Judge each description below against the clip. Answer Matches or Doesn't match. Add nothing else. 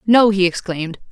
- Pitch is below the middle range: Doesn't match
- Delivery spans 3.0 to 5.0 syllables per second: Doesn't match